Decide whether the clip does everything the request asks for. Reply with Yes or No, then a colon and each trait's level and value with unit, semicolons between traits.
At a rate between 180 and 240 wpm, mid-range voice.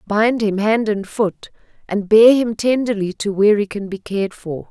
No: fast, 205 wpm; high, 210 Hz